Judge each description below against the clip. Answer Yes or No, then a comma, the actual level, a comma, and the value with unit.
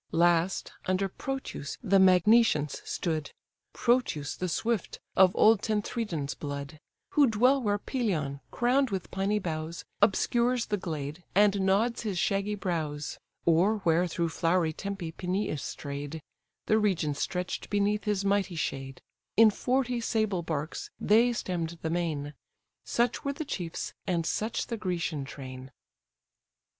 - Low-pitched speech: No, medium, 185 Hz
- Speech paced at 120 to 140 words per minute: Yes, slow, 135 wpm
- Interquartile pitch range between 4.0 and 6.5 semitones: Yes, average, 5.0 semitones